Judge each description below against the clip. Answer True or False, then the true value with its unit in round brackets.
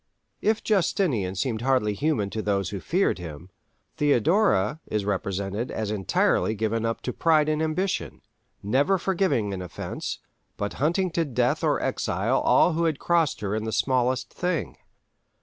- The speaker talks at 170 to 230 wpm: False (155 wpm)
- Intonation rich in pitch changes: True (8.1 semitones)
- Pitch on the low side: True (125 Hz)